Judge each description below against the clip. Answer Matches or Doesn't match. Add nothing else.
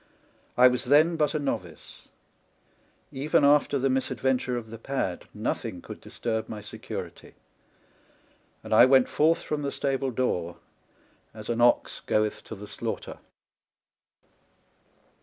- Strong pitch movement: Doesn't match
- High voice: Doesn't match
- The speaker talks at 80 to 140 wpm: Matches